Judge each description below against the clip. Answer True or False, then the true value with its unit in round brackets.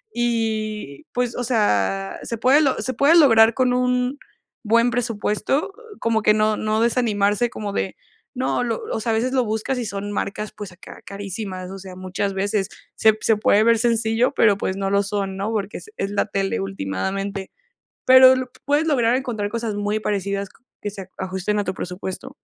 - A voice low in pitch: False (215 Hz)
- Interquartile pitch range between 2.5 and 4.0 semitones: True (3.5 semitones)